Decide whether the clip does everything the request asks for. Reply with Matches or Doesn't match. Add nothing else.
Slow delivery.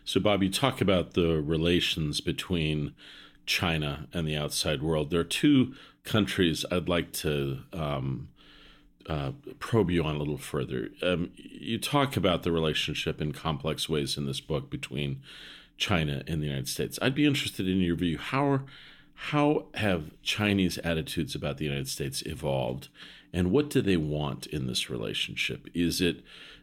Doesn't match